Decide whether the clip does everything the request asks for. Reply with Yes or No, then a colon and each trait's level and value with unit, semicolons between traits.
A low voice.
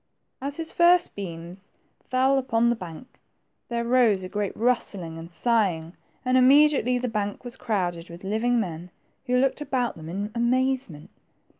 No: high, 230 Hz